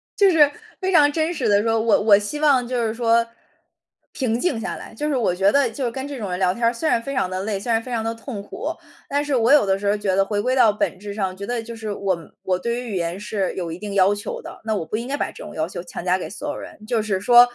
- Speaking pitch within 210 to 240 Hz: Yes, high, 225 Hz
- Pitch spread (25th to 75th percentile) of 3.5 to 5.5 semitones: Yes, average, 4.3 semitones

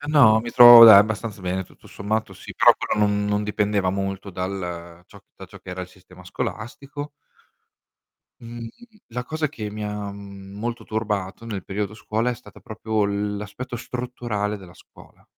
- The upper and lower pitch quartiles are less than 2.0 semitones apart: No, average, 2.8 semitones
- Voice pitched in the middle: No, low, 105 Hz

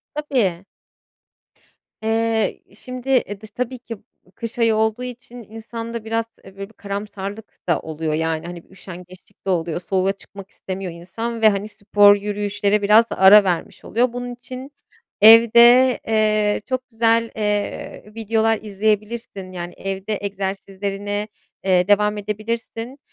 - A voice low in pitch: No, high, 210 Hz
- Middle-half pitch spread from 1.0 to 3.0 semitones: Yes, average, 2.7 semitones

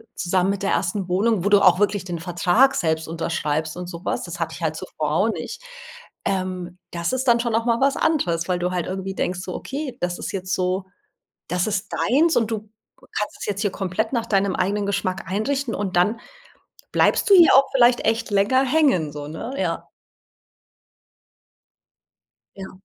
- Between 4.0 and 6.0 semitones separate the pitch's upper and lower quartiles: Yes, average, 4.4 semitones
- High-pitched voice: Yes, high, 195 Hz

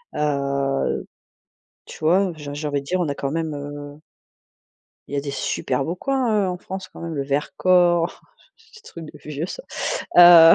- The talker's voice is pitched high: No, medium, 160 Hz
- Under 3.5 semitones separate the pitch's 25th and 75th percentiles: No, average, 3.9 semitones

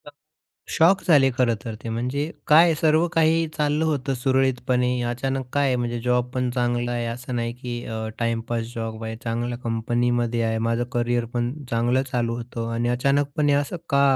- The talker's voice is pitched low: Yes, low, 120 Hz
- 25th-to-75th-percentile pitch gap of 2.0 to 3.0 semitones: Yes, average, 2.7 semitones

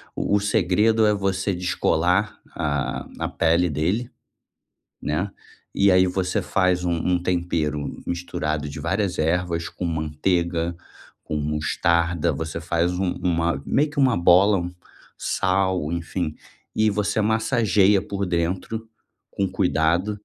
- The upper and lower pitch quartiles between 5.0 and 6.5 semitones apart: No, average, 2.9 semitones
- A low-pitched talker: Yes, very low, 90 Hz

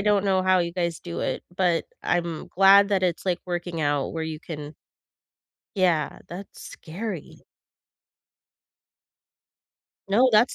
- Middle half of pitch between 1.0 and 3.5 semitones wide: Yes, average, 2.8 semitones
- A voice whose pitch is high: No, medium, 175 Hz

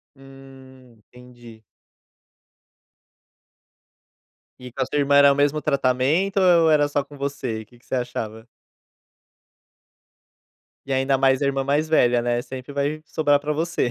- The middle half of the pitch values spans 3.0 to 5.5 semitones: No, narrow, 2.5 semitones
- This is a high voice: No, low, 135 Hz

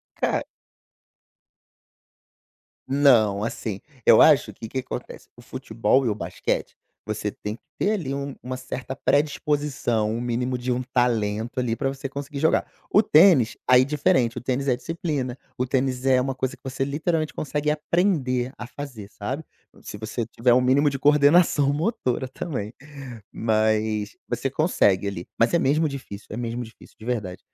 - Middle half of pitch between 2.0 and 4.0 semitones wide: Yes, average, 3.6 semitones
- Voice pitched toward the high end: No, low, 130 Hz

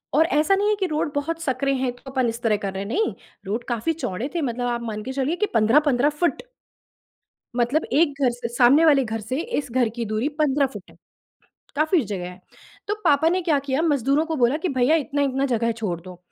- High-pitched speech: Yes, very high, 270 Hz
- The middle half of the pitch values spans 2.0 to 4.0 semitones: No, average, 4.6 semitones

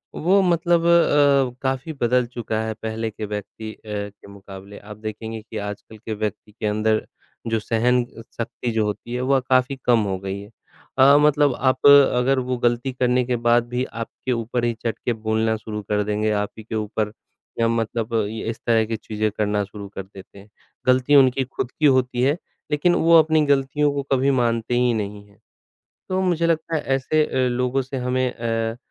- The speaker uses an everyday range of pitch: Yes, average, 3.6 semitones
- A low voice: Yes, low, 120 Hz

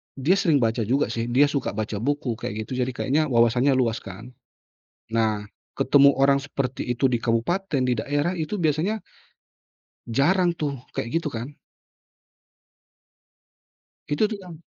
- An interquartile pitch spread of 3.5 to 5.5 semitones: Yes, average, 4.1 semitones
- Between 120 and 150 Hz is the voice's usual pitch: Yes, low, 135 Hz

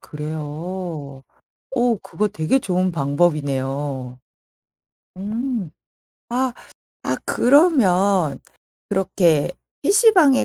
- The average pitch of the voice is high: No, medium, 180 Hz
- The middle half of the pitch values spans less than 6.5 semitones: No, wide, 8.2 semitones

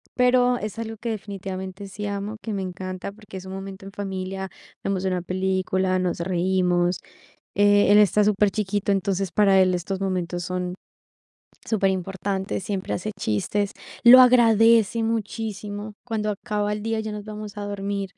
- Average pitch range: No, narrow, 2.0 semitones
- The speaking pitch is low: No, high, 200 Hz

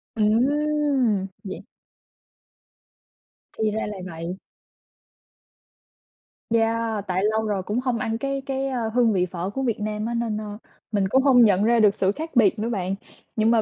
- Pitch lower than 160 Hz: No, high, 220 Hz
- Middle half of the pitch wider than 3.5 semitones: No, average, 3.0 semitones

